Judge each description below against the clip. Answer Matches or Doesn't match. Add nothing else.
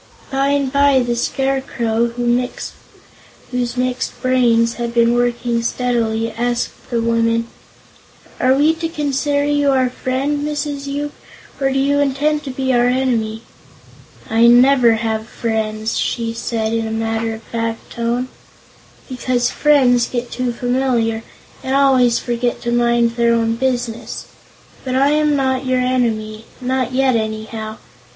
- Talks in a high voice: Matches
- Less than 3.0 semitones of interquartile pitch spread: Matches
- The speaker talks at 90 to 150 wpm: Matches